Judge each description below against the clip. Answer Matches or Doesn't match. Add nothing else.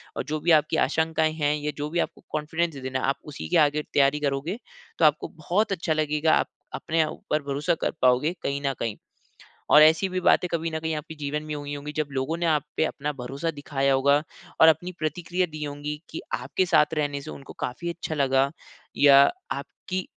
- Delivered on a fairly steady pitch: Matches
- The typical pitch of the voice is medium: Matches